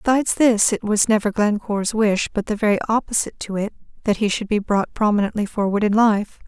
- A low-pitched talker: No, high, 210 Hz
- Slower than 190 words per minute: No, fast, 205 wpm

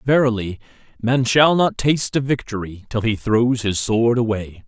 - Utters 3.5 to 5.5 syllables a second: Yes, 4.7 syllables/s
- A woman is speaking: No, male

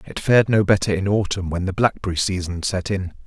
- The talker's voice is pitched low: Yes, very low, 95 Hz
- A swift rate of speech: Yes, fast, 220 wpm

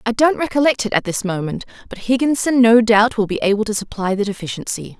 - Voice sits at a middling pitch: No, high, 215 Hz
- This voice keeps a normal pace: No, fast, 215 wpm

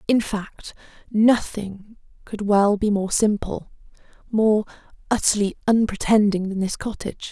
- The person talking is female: Yes, female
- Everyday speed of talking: No, slow, 105 wpm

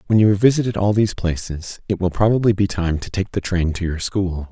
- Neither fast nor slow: No, fast, 250 wpm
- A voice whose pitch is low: Yes, very low, 95 Hz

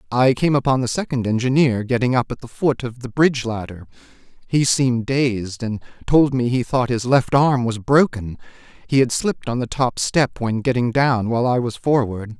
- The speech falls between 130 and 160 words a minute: No, fast, 205 wpm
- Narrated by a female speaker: No, male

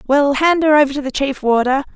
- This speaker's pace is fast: Yes, fast, 245 wpm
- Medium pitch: No, very high, 280 Hz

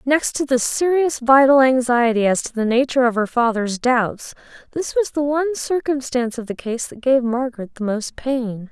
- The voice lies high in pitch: Yes, very high, 255 Hz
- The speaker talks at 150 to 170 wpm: No, average, 195 wpm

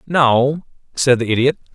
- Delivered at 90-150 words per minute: Yes, average, 140 wpm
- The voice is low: Yes, low, 130 Hz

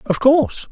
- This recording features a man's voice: Yes, male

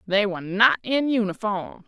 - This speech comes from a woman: Yes, female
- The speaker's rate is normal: Yes, average, 160 wpm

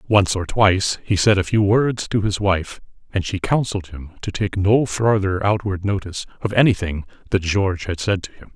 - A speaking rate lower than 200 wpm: No, fast, 205 wpm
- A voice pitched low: Yes, low, 100 Hz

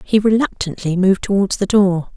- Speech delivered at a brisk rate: No, average, 165 wpm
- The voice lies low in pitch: No, high, 195 Hz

